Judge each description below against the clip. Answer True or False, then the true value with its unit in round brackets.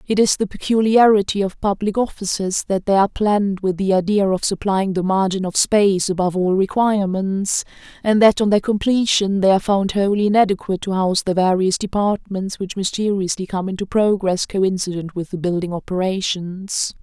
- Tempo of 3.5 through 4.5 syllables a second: False (5.4 syllables/s)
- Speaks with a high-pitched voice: True (195 Hz)